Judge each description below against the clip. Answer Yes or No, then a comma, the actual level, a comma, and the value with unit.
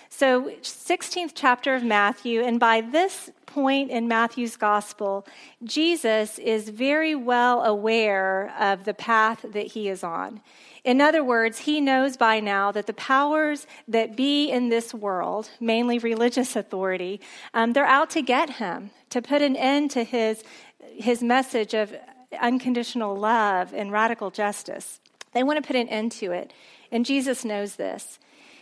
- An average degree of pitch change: Yes, average, 3.8 semitones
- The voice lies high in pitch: Yes, high, 235 Hz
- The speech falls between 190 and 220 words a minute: No, average, 155 wpm